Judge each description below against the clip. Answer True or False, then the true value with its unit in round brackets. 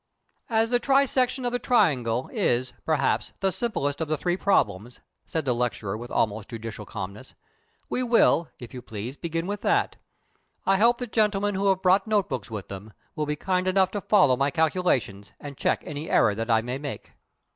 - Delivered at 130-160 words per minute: False (190 wpm)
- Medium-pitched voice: True (150 Hz)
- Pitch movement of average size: False (9.0 semitones)